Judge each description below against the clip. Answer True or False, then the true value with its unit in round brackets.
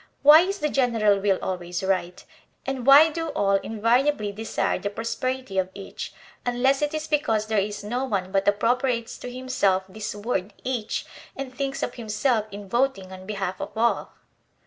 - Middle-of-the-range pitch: False (225 Hz)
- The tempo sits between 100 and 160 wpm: False (170 wpm)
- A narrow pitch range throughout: False (4.8 semitones)